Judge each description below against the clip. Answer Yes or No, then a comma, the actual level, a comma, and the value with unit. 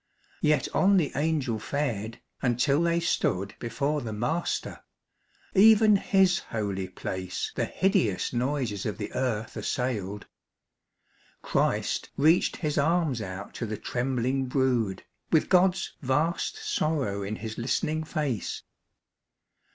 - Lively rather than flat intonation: Yes, wide, 6.6 semitones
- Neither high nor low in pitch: No, low, 130 Hz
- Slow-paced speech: Yes, slow, 120 wpm